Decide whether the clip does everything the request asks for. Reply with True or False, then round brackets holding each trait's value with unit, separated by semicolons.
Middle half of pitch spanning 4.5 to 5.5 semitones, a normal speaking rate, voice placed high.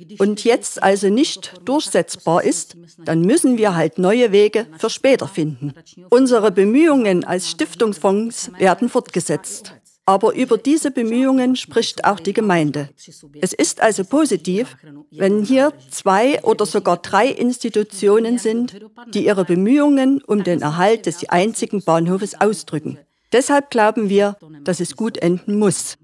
True (5.1 semitones; 135 wpm; 205 Hz)